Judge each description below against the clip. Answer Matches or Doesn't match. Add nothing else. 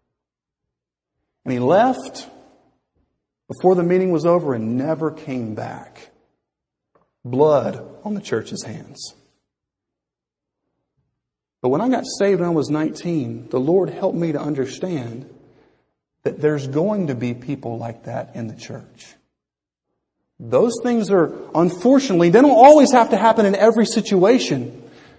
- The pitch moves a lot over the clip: Matches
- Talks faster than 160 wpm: Doesn't match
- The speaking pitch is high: Doesn't match